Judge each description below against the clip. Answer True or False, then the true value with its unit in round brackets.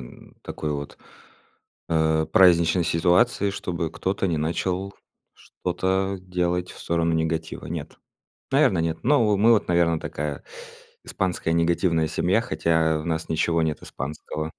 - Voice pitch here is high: False (85 Hz)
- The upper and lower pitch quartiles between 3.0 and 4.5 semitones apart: False (2.5 semitones)